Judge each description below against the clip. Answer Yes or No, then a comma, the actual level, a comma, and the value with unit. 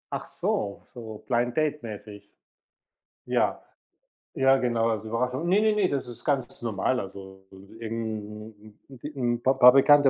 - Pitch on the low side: Yes, low, 120 Hz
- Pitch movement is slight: No, average, 3.8 semitones